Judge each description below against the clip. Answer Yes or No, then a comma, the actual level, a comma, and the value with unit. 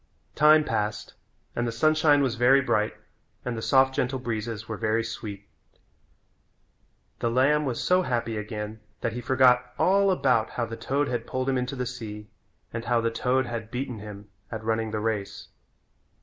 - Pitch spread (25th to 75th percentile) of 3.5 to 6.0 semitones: No, average, 2.9 semitones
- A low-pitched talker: Yes, low, 120 Hz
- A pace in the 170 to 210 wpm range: Yes, average, 175 wpm